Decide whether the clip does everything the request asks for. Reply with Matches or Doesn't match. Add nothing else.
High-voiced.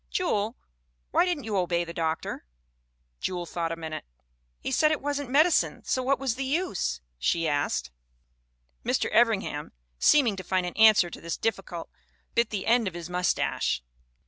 Matches